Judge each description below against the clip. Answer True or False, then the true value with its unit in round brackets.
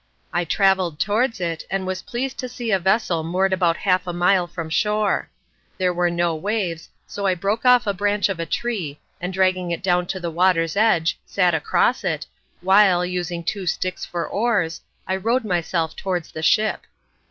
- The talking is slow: False (185 wpm)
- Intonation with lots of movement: False (2.9 semitones)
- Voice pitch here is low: False (185 Hz)